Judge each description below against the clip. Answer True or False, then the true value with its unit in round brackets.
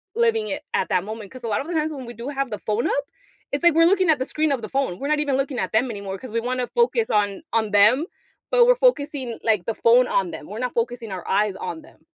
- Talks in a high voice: True (255 Hz)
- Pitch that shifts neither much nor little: False (5.9 semitones)